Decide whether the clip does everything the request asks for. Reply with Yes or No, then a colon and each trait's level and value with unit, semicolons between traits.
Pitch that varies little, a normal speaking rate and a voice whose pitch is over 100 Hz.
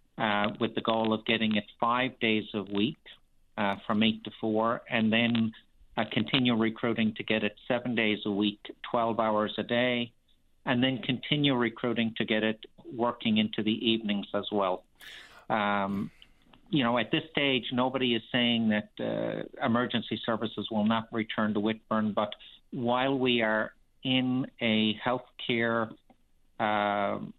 Yes: narrow, 2.0 semitones; average, 160 wpm; low, 115 Hz